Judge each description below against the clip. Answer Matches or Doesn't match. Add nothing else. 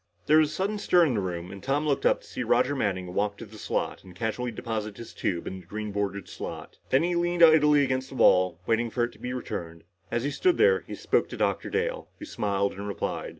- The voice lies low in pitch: Matches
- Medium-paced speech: Doesn't match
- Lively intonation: Matches